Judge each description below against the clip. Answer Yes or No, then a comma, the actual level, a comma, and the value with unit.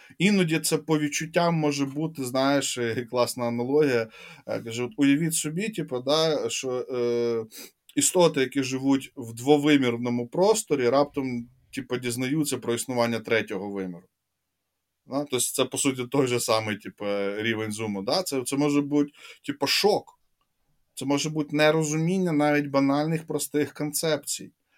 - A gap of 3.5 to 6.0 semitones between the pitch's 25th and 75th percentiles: Yes, average, 3.9 semitones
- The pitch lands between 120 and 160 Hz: Yes, low, 135 Hz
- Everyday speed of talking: Yes, average, 135 wpm